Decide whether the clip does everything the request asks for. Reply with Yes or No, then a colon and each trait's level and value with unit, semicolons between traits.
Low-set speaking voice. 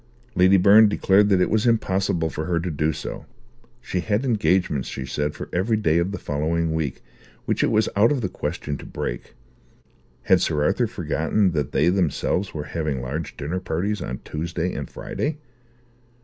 Yes: very low, 90 Hz